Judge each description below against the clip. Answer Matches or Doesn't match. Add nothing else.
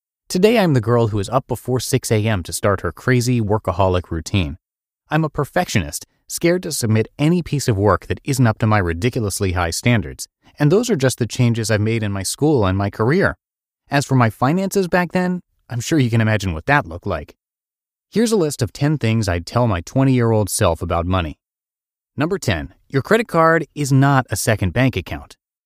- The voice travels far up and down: Matches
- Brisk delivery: Matches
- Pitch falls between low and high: Doesn't match